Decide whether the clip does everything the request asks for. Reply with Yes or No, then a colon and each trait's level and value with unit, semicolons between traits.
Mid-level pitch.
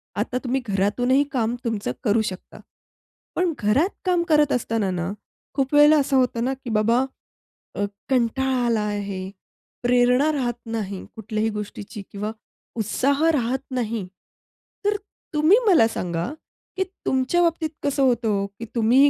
No: high, 240 Hz